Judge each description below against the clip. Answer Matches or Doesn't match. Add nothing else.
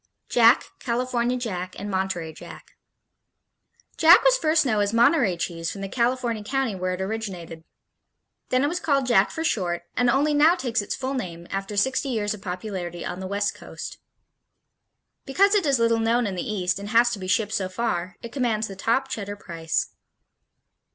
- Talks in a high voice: Matches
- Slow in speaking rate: Doesn't match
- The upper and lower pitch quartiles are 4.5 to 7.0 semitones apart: Matches